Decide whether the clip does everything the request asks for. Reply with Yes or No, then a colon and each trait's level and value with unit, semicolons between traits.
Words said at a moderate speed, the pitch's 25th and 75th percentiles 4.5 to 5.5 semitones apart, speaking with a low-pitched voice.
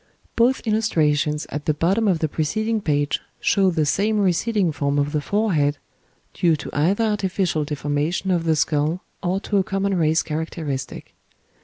No: average, 160 wpm; average, 4.9 semitones; medium, 165 Hz